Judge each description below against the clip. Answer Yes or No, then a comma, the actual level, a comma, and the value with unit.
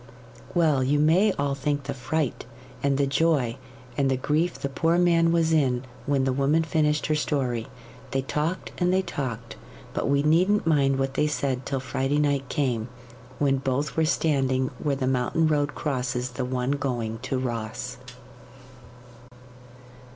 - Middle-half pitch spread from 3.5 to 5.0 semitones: No, average, 2.9 semitones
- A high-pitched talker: No, medium, 140 Hz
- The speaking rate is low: No, average, 160 wpm